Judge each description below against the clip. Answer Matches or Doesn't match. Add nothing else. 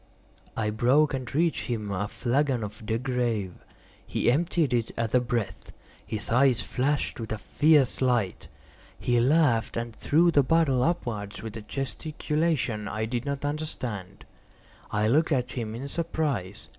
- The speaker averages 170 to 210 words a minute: Doesn't match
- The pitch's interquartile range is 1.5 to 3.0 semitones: Doesn't match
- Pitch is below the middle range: Matches